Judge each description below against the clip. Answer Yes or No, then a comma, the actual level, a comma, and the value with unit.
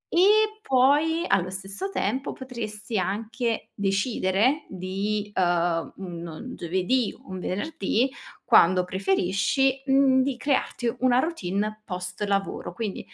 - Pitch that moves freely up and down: Yes, wide, 5.8 semitones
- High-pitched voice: Yes, high, 210 Hz